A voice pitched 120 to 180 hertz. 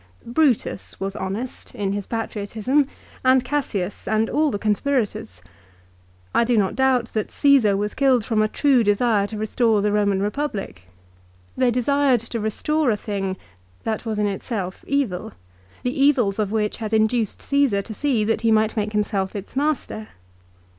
No: high, 220 Hz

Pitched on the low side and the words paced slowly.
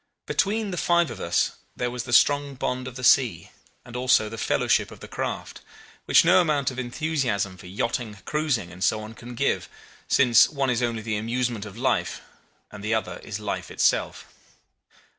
No: low, 120 Hz; average, 185 wpm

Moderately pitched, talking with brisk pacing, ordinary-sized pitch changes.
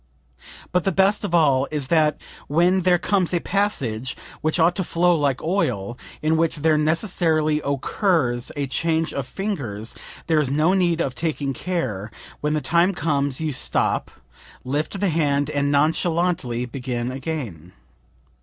No: medium, 155 Hz; average, 155 wpm; average, 4.2 semitones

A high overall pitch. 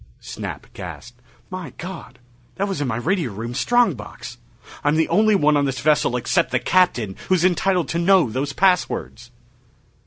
No: medium, 155 Hz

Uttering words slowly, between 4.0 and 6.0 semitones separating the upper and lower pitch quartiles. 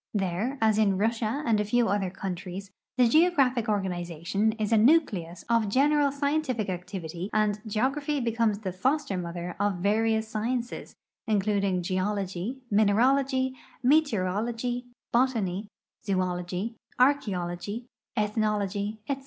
Yes: slow, 115 wpm; average, 4.4 semitones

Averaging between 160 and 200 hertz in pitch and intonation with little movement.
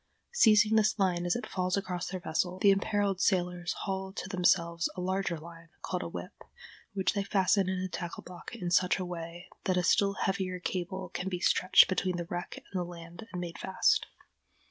Yes: medium, 185 Hz; narrow, 1.6 semitones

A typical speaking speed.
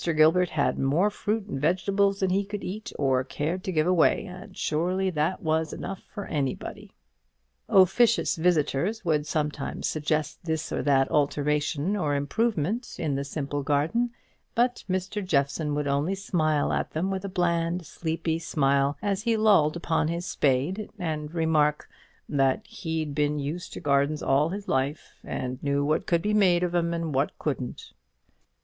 Yes: average, 165 wpm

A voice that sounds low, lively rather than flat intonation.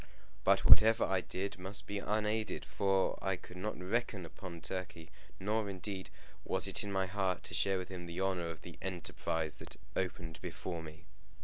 No: very low, 95 Hz; narrow, 2.5 semitones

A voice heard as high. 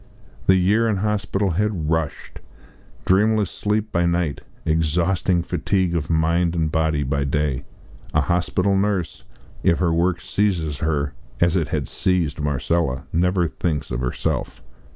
No: very low, 85 Hz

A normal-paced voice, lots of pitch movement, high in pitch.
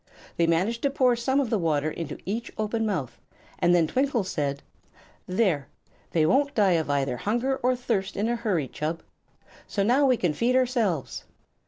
Yes: average, 180 wpm; wide, 6.8 semitones; high, 205 Hz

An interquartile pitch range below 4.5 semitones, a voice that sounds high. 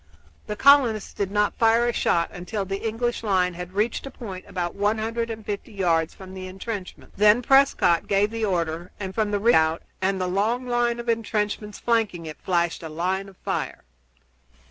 Yes: average, 3.7 semitones; high, 205 Hz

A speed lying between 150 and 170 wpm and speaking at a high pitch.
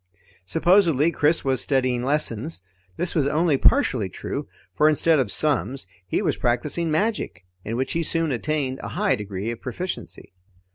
No: average, 155 wpm; medium, 145 Hz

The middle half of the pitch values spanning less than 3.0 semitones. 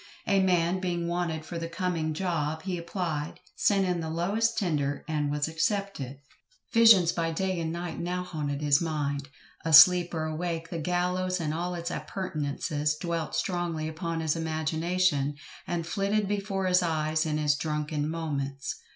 Yes: narrow, 2.6 semitones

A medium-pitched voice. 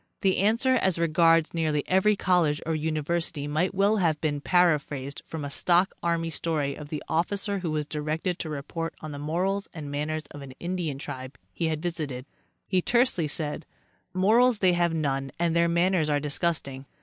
Yes: medium, 165 Hz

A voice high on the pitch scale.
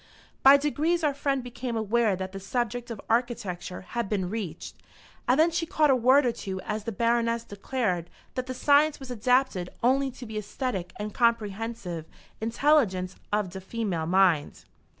Yes: high, 230 Hz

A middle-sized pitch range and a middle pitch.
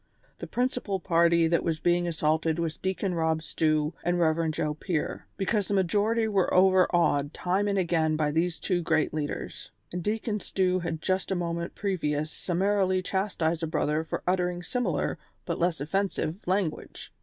Yes: average, 3.0 semitones; medium, 175 Hz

